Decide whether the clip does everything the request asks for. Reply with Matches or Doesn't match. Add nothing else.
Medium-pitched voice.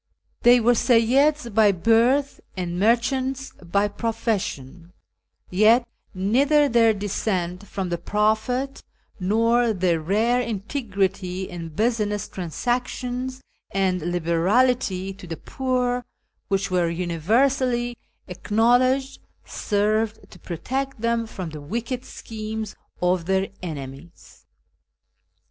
Doesn't match